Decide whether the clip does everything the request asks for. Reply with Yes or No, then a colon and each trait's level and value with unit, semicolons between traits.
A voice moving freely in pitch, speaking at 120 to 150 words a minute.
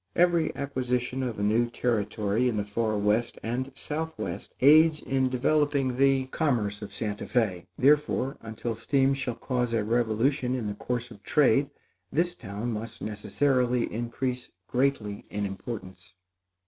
No: average, 4.1 semitones; average, 145 wpm